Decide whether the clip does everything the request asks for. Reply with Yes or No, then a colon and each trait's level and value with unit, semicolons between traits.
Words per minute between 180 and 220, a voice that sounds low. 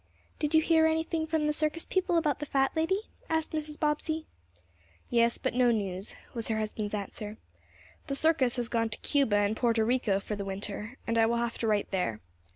No: average, 200 wpm; high, 245 Hz